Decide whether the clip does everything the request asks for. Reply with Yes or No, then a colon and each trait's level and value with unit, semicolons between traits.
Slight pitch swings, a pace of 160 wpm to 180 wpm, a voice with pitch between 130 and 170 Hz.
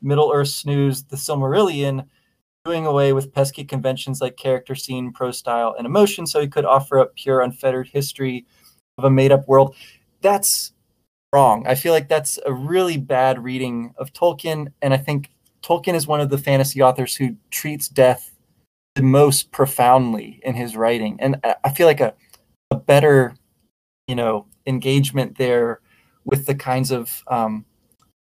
Yes: narrow, 1.9 semitones; average, 165 wpm; low, 135 Hz